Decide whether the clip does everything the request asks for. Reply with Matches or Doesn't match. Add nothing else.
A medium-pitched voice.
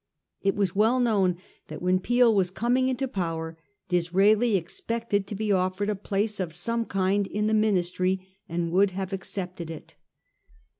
Doesn't match